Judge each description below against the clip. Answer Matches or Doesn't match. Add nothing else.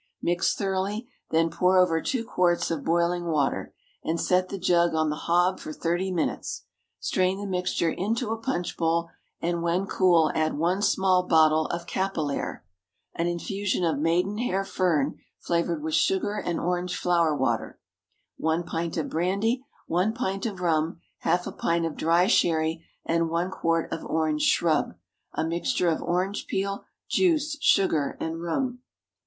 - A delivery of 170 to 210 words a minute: Doesn't match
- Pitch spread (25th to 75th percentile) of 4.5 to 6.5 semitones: Doesn't match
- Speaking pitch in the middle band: Matches